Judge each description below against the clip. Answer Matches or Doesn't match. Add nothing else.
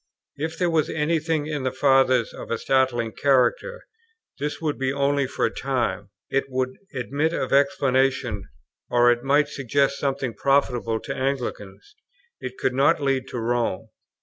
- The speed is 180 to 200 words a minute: Doesn't match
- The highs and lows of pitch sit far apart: Doesn't match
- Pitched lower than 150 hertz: Matches